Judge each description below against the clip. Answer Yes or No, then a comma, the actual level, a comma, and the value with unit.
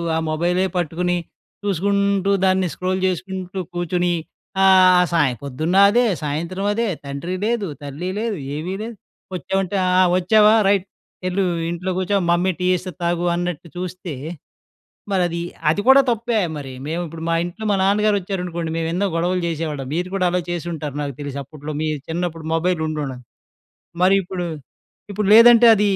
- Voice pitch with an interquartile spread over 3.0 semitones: No, average, 2.7 semitones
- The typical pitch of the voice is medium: Yes, medium, 180 Hz